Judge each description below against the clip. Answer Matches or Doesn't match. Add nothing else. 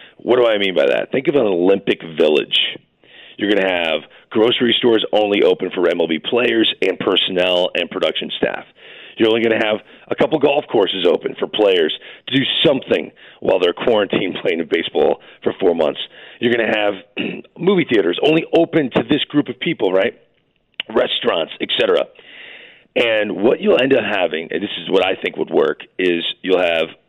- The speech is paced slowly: Doesn't match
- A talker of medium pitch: Doesn't match